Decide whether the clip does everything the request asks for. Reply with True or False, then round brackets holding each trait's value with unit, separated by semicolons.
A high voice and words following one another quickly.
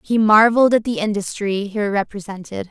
False (210 Hz; 155 wpm)